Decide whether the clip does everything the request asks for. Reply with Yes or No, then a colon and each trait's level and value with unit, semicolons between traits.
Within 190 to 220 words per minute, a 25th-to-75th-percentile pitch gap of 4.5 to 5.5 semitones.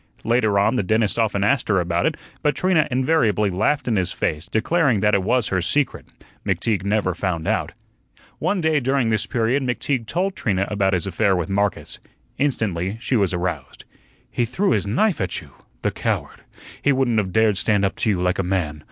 Yes: average, 195 wpm; average, 5.1 semitones